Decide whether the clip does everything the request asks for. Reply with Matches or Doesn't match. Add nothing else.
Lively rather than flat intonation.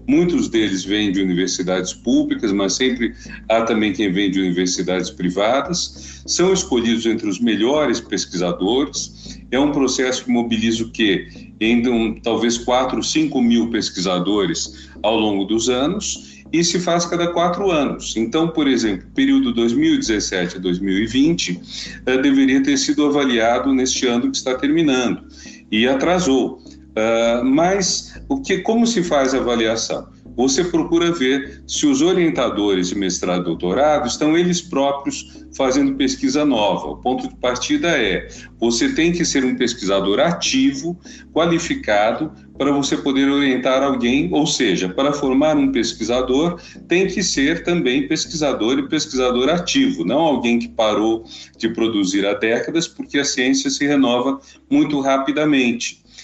Matches